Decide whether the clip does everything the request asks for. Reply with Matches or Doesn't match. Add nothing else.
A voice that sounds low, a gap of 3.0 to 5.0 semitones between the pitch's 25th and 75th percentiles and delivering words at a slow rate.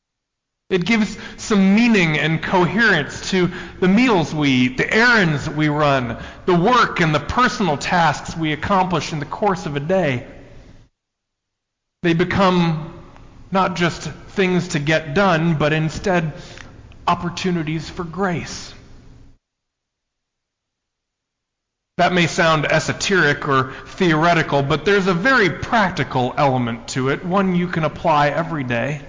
Doesn't match